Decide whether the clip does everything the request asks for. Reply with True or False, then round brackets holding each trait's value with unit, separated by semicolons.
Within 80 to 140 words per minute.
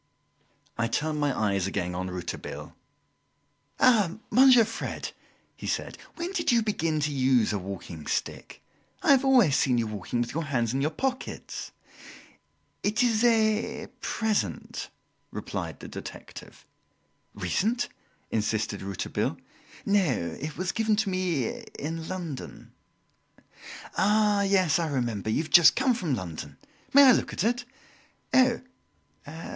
True (135 wpm)